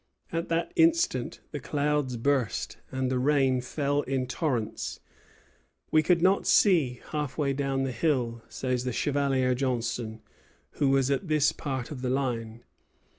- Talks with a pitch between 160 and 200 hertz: No, low, 135 Hz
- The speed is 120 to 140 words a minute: No, average, 150 wpm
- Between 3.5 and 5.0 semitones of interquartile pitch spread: No, average, 2.8 semitones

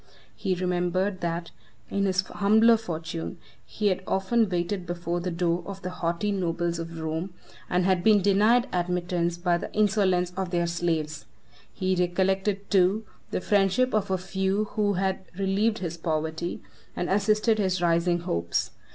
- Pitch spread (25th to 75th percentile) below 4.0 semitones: Yes, narrow, 2.5 semitones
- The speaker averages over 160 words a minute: No, average, 155 wpm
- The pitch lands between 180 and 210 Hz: Yes, medium, 185 Hz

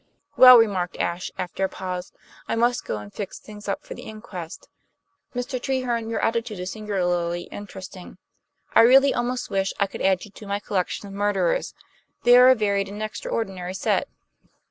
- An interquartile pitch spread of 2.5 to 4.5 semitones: Yes, average, 3.7 semitones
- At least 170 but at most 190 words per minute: Yes, average, 175 wpm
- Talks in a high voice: Yes, high, 205 Hz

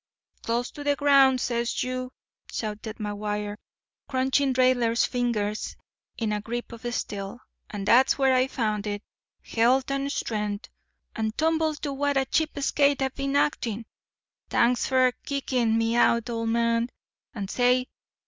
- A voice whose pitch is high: Yes, high, 240 Hz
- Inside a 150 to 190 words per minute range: No, average, 140 wpm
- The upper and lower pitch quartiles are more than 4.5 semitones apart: No, average, 3.2 semitones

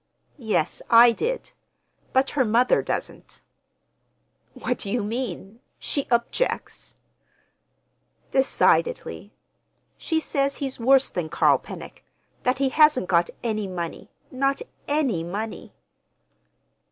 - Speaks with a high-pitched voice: Yes, high, 245 Hz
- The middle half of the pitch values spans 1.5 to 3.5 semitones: No, average, 4.5 semitones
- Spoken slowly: Yes, slow, 95 wpm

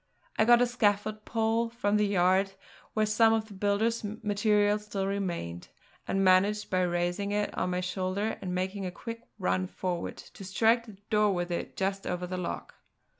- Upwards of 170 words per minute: Yes, average, 180 wpm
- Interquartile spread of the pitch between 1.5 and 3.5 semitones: Yes, narrow, 2.6 semitones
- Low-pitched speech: No, high, 200 Hz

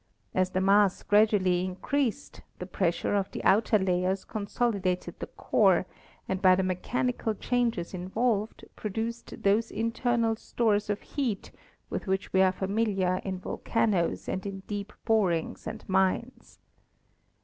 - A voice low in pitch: No, high, 200 Hz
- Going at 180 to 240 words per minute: No, slow, 135 wpm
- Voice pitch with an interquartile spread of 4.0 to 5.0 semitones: No, average, 3.2 semitones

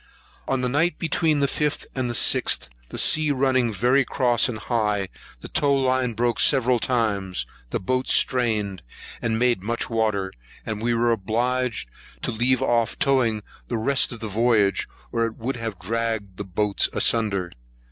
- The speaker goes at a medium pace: Yes, average, 165 wpm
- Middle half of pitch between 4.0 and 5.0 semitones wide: No, average, 3.1 semitones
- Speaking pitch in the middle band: No, low, 115 Hz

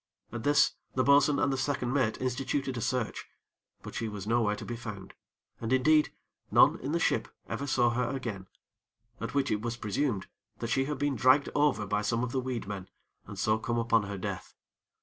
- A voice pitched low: Yes, low, 120 Hz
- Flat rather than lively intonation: No, average, 3.7 semitones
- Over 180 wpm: Yes, fast, 205 wpm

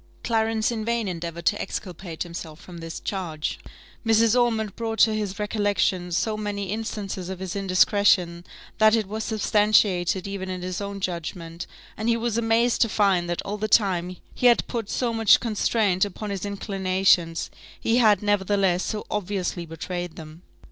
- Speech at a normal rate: Yes, average, 165 wpm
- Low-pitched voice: No, high, 200 Hz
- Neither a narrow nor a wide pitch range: Yes, average, 3.4 semitones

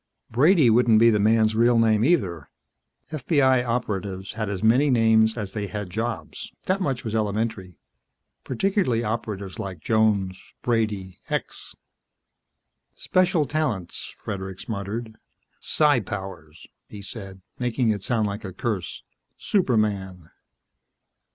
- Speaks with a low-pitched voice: Yes, low, 110 Hz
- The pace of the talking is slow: Yes, slow, 120 wpm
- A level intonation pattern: No, average, 3.5 semitones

